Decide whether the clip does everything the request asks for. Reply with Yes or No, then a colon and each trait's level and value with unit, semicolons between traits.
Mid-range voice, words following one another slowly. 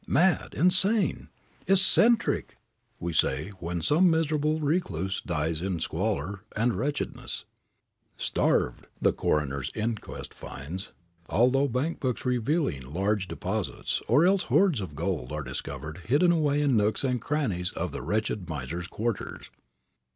No: low, 110 Hz; slow, 130 wpm